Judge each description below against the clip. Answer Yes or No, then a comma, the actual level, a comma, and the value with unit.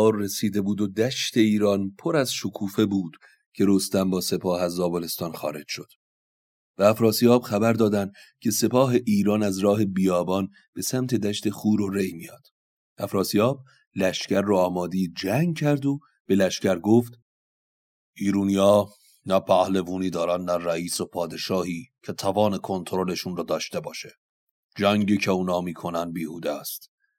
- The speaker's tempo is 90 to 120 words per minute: No, average, 140 wpm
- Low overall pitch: Yes, low, 100 Hz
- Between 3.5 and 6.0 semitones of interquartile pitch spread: No, average, 2.8 semitones